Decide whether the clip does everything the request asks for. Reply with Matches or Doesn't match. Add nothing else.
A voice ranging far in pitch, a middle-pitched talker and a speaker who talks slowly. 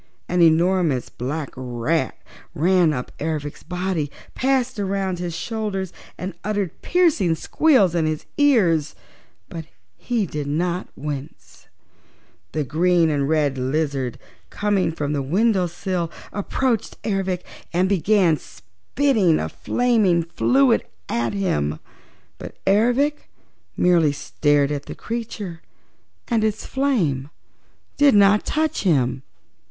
Matches